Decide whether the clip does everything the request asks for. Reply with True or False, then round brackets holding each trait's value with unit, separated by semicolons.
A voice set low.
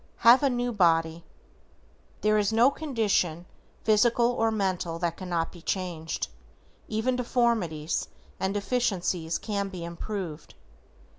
False (200 Hz)